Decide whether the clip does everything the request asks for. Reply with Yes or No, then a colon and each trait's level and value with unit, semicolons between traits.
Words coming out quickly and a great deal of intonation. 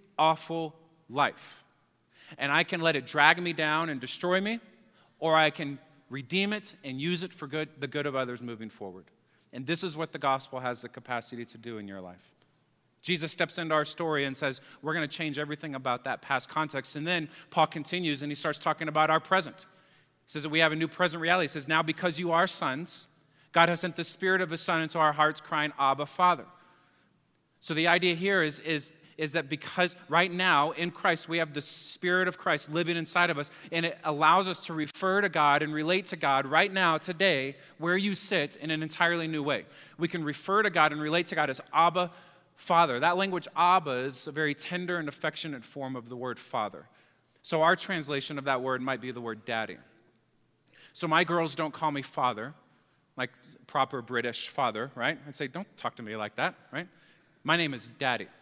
No: fast, 215 wpm; average, 3.5 semitones